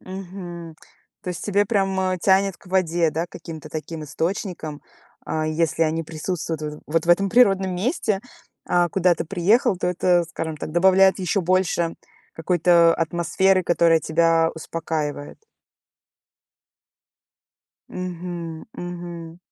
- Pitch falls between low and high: Yes, medium, 175 Hz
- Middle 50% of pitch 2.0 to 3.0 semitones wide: Yes, narrow, 2.4 semitones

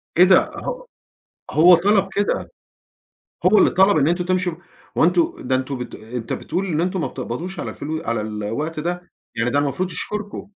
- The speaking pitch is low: No, medium, 170 Hz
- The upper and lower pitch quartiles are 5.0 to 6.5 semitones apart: Yes, wide, 5.4 semitones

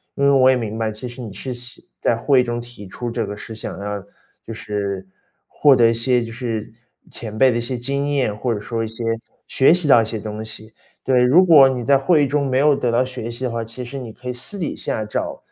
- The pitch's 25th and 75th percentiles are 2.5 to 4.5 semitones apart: Yes, average, 2.9 semitones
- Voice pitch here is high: No, low, 120 Hz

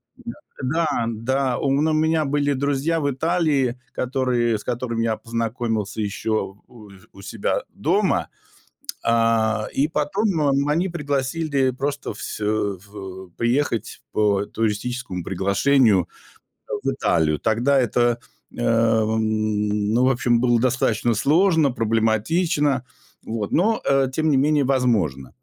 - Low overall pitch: Yes, low, 120 Hz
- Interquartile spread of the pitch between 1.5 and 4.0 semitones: No, average, 4.5 semitones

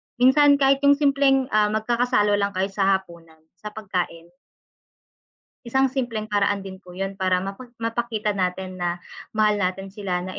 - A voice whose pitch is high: Yes, high, 205 Hz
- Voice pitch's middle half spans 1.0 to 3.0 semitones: No, average, 4.1 semitones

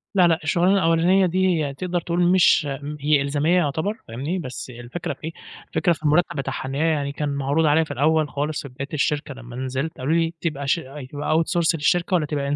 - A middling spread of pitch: Yes, average, 3.3 semitones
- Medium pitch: Yes, medium, 155 Hz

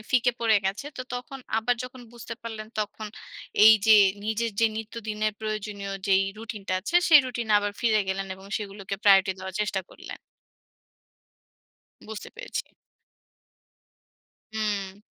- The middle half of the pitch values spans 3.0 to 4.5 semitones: No, narrow, 2.5 semitones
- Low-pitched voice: No, high, 215 Hz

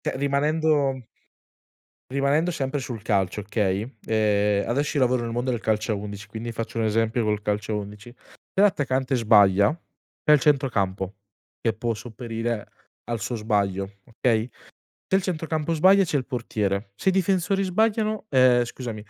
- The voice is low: Yes, low, 120 Hz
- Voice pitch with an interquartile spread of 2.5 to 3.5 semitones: No, average, 5.1 semitones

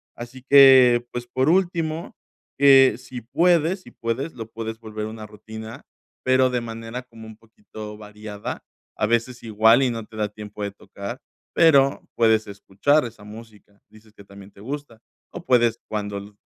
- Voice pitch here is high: No, low, 115 Hz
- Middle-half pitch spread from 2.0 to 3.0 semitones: No, average, 3.4 semitones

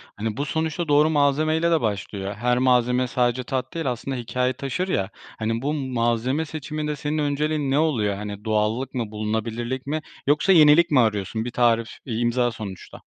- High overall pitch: No, low, 125 Hz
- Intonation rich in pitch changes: No, average, 4.8 semitones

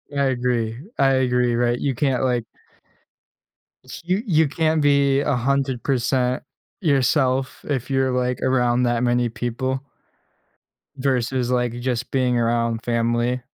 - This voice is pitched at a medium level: No, low, 125 Hz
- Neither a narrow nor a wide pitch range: No, narrow, 2.0 semitones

